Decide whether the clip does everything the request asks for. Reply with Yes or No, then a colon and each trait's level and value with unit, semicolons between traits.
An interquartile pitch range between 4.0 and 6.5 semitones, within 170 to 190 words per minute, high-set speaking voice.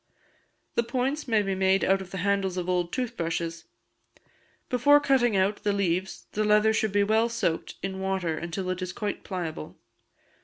No: average, 3.2 semitones; average, 180 wpm; high, 195 Hz